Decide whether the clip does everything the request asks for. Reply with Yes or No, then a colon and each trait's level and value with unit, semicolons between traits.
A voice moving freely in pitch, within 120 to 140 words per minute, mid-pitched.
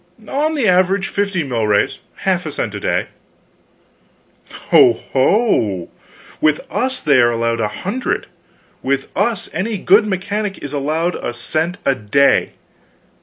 Yes: wide, 8.4 semitones; slow, 135 wpm; medium, 160 Hz